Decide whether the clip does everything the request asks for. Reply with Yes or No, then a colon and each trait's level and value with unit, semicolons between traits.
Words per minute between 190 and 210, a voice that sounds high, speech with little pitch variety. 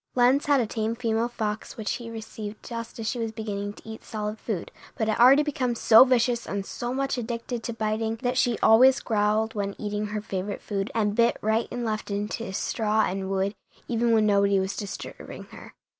Yes: fast, 205 wpm; high, 220 Hz; narrow, 2.1 semitones